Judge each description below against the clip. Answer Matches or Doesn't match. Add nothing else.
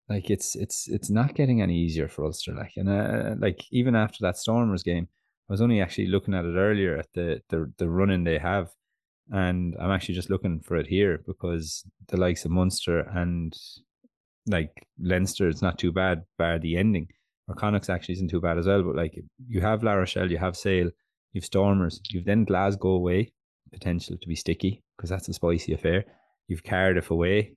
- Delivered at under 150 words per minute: Doesn't match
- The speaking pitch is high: Doesn't match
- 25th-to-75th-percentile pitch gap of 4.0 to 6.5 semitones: Doesn't match